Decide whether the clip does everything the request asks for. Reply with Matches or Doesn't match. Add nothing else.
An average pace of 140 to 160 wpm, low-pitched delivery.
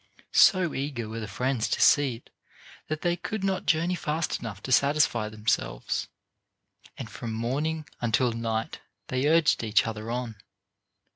Matches